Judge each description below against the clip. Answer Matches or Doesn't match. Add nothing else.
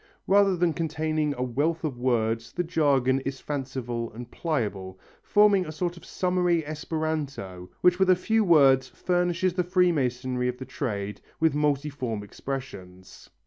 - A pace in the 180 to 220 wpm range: Doesn't match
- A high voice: Doesn't match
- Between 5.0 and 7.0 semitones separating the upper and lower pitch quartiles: Matches